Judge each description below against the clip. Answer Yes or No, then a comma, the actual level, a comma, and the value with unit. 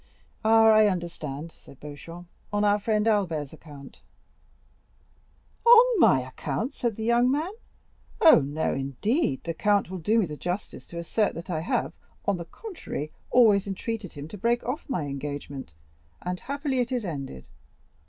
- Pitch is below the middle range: No, high, 190 Hz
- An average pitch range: No, wide, 7.2 semitones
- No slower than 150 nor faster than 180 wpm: Yes, average, 160 wpm